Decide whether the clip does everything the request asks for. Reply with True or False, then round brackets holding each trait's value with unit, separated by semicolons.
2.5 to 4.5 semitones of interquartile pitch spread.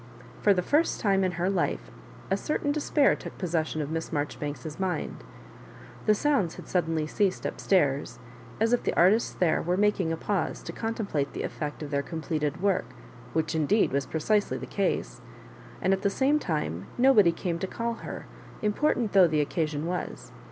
False (5.0 semitones)